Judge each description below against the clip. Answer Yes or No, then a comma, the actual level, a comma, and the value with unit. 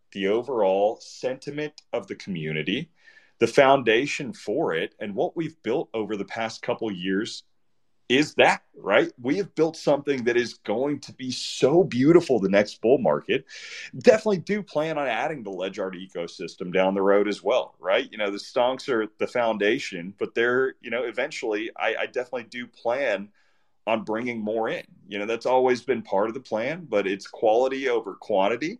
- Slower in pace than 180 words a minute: No, average, 185 wpm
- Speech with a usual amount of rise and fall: No, wide, 7.6 semitones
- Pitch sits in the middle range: No, low, 125 Hz